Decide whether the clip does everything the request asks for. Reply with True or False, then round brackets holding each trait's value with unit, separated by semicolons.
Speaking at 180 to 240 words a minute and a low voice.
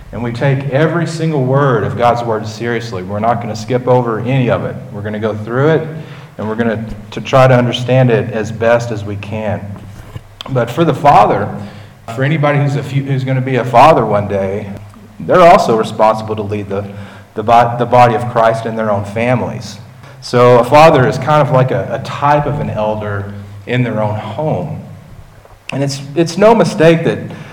True (205 wpm; 120 Hz)